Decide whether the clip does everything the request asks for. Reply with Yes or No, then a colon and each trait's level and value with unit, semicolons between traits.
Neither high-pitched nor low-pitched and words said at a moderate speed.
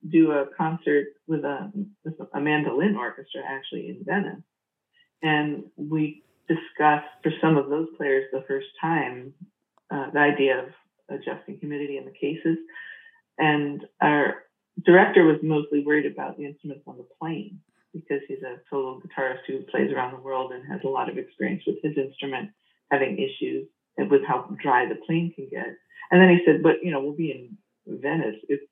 Yes: medium, 155 Hz; average, 180 wpm